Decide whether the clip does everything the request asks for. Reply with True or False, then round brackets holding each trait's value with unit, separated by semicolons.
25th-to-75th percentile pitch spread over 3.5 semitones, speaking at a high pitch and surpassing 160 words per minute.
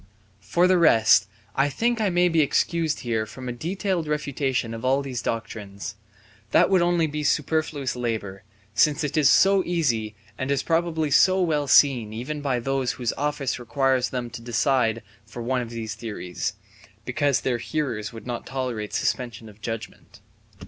False (5.0 semitones; 130 Hz; 170 wpm)